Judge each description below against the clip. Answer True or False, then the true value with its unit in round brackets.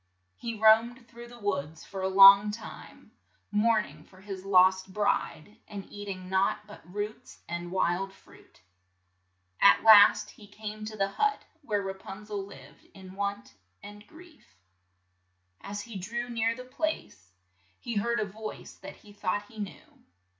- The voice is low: False (205 Hz)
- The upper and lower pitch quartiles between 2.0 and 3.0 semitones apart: True (2.4 semitones)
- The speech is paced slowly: False (160 wpm)